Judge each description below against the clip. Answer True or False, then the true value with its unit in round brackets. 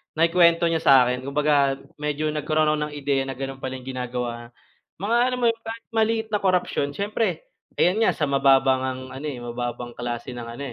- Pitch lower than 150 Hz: True (140 Hz)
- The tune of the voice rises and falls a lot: False (4.6 semitones)